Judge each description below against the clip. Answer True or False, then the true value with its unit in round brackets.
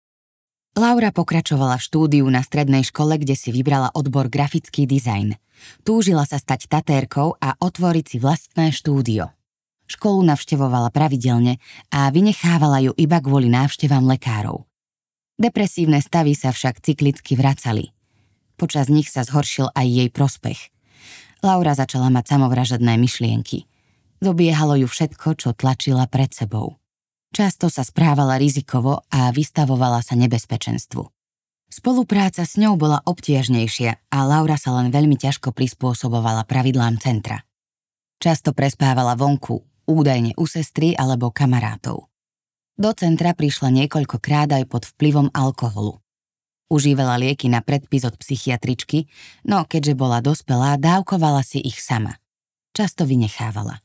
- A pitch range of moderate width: True (3.6 semitones)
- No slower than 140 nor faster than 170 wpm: False (125 wpm)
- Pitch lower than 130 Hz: False (135 Hz)